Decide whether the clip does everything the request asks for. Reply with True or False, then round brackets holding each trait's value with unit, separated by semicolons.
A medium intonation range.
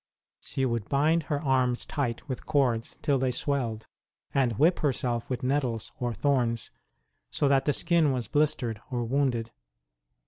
True (3.3 semitones)